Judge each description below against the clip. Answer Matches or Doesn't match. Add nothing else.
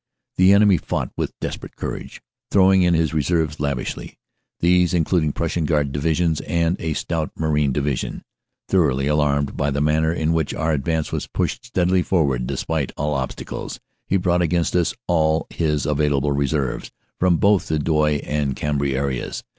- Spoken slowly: Doesn't match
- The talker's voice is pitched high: Doesn't match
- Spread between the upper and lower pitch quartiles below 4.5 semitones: Matches